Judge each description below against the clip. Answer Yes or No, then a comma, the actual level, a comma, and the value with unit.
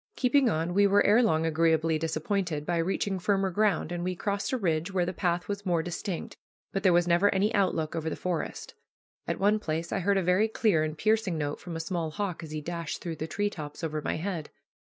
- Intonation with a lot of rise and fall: No, average, 3.7 semitones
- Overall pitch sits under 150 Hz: No, medium, 175 Hz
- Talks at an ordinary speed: No, fast, 230 wpm